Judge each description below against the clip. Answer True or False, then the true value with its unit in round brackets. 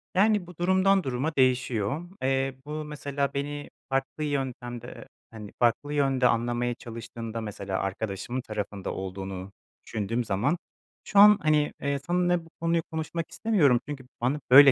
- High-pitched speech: False (135 Hz)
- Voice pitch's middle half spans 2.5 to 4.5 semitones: False (4.9 semitones)